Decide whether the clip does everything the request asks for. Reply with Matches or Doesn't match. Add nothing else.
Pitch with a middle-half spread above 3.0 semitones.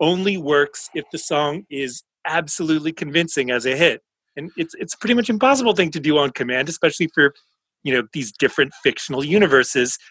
Matches